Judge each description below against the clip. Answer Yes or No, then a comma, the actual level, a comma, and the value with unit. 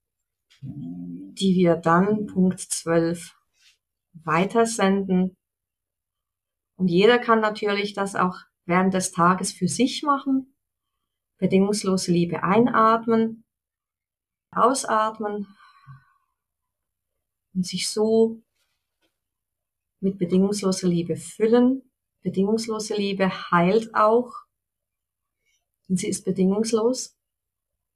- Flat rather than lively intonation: No, average, 3.8 semitones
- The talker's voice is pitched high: Yes, high, 195 Hz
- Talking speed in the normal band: No, slow, 80 wpm